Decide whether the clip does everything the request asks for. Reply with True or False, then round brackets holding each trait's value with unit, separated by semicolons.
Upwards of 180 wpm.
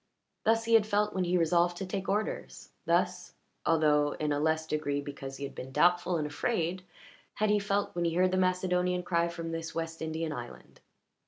True (195 wpm)